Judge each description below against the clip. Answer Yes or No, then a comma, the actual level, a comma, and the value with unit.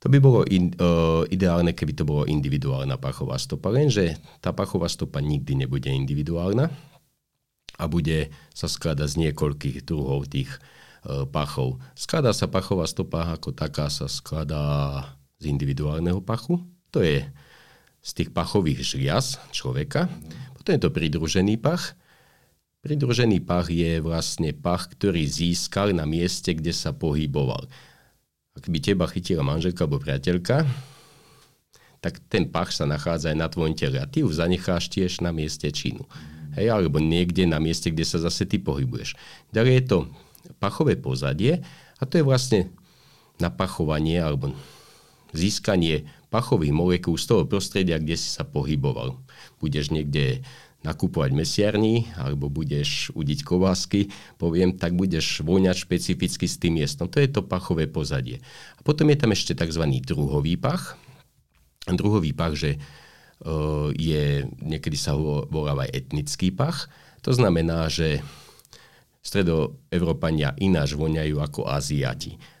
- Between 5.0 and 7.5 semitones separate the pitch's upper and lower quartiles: Yes, wide, 5.6 semitones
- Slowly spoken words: No, average, 135 wpm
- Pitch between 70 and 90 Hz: Yes, very low, 85 Hz